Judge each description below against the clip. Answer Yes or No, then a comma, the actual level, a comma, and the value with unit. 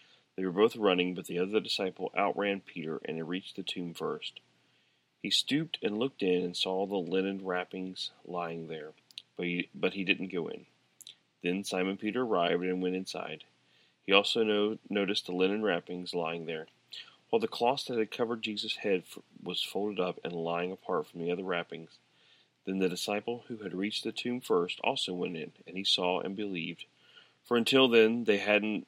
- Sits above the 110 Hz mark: No, very low, 95 Hz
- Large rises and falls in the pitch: No, average, 2.9 semitones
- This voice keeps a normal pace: Yes, average, 190 wpm